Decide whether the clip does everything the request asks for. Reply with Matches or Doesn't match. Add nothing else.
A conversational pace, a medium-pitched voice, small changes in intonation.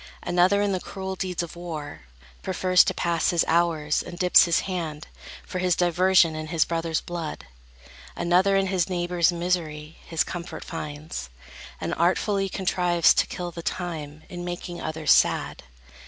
Matches